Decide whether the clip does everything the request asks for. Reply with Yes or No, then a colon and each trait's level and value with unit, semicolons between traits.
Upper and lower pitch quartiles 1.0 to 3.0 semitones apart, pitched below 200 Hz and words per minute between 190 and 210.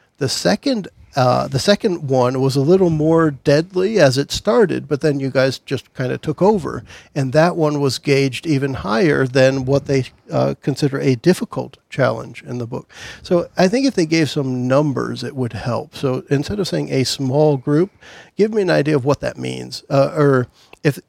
No: average, 3.7 semitones; medium, 140 Hz; average, 200 wpm